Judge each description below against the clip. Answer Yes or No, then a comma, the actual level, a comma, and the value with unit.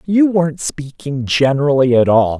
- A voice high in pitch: No, medium, 145 Hz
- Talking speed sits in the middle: Yes, average, 150 wpm